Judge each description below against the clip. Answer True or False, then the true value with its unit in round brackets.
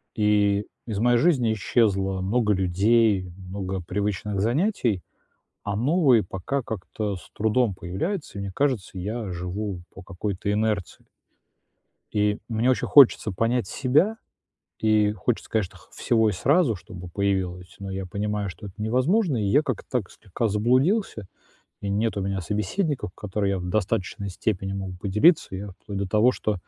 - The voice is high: False (105 Hz)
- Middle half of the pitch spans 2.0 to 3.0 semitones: False (3.4 semitones)